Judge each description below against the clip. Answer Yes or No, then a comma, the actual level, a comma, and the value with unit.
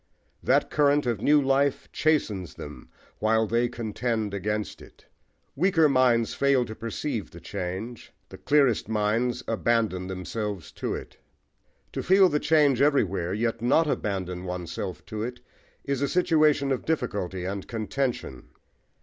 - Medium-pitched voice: No, low, 115 Hz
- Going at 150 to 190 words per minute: No, average, 140 wpm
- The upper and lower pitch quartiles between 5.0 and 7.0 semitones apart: Yes, wide, 5.6 semitones